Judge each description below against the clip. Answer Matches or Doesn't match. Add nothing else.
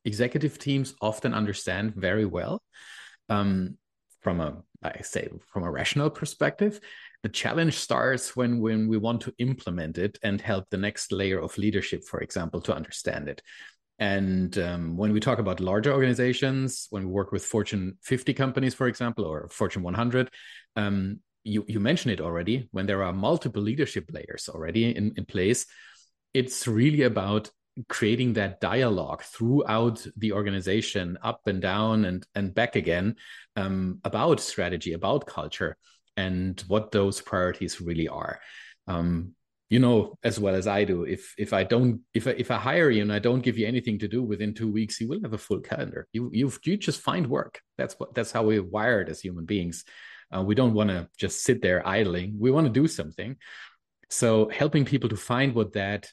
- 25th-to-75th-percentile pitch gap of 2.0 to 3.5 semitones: Doesn't match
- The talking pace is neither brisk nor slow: Matches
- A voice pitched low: Matches